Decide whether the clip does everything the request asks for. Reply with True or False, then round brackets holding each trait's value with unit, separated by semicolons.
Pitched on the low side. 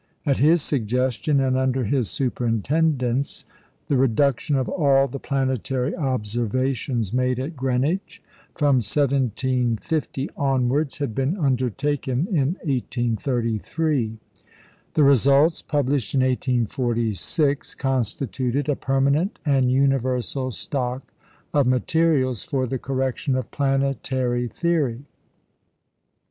True (130 Hz)